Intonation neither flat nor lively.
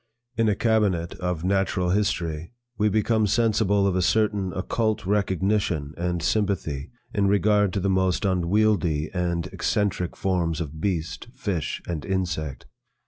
Yes: average, 3.3 semitones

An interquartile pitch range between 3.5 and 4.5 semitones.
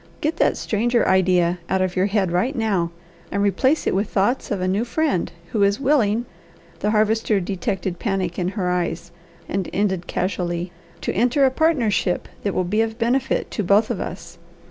Yes: average, 3.8 semitones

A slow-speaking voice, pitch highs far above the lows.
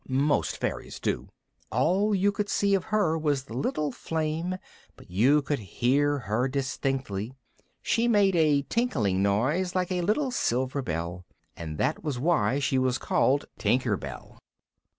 No: average, 150 wpm; wide, 6.4 semitones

